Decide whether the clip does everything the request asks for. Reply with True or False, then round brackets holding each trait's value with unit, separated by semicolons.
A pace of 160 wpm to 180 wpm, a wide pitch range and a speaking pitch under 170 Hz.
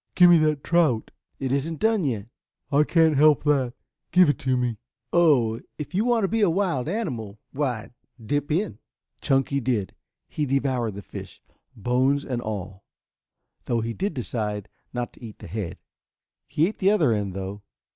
True (175 wpm; 6.2 semitones; 135 Hz)